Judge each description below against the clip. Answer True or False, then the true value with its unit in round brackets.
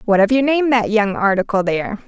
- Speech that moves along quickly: True (230 wpm)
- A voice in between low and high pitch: False (220 Hz)